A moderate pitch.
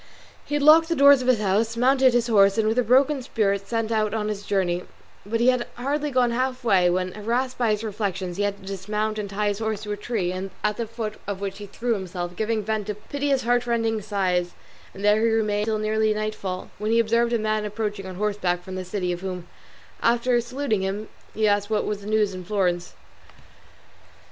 No: high, 215 Hz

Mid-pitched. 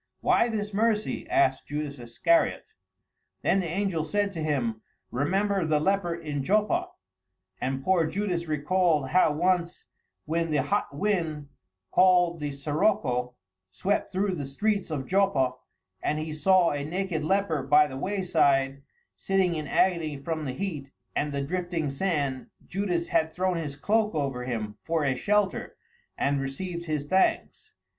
Yes: medium, 165 Hz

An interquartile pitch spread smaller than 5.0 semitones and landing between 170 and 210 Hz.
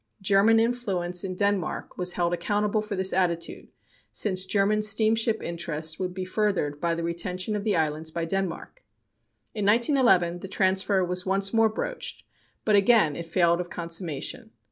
Yes: average, 3.6 semitones; high, 190 Hz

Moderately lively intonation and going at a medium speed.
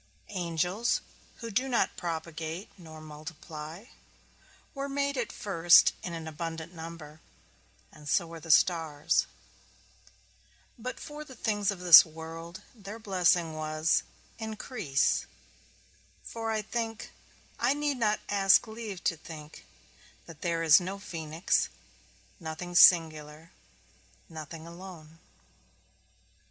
No: average, 4.8 semitones; slow, 110 wpm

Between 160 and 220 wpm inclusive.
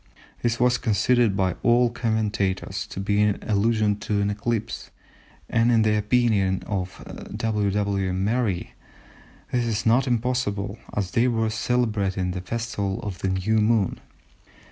No: average, 145 wpm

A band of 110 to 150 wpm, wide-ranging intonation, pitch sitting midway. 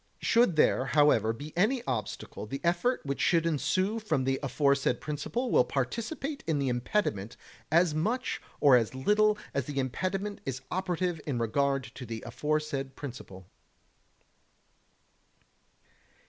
Yes: slow, 135 wpm; wide, 6.0 semitones; medium, 150 Hz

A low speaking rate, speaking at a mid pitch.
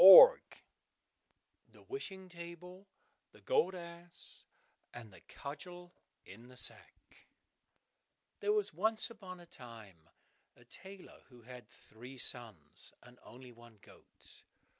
Yes: slow, 120 wpm; medium, 170 Hz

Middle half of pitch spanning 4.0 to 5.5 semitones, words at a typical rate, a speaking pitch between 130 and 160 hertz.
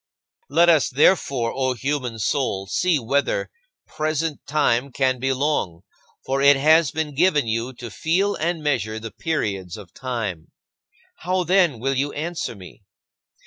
Yes: average, 5.2 semitones; average, 150 wpm; low, 135 Hz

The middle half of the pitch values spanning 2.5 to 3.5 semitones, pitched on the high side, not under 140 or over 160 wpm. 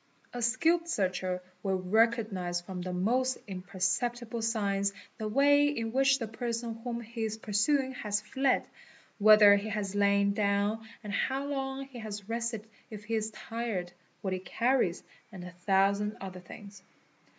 Yes: average, 3.2 semitones; high, 215 Hz; average, 155 wpm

